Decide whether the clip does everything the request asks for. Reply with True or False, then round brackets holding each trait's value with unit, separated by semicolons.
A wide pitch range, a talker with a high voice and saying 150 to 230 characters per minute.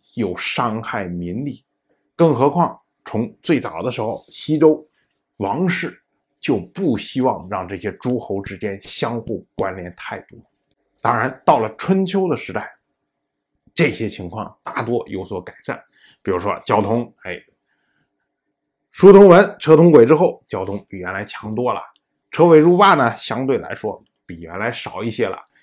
False (8.5 semitones; 135 Hz; 215 characters per minute)